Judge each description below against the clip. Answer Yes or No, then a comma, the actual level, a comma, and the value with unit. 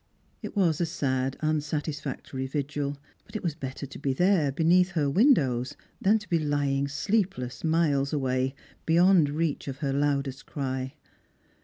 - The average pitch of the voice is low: No, medium, 145 Hz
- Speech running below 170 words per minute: Yes, average, 150 wpm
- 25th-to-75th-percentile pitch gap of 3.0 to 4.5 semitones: Yes, average, 3.4 semitones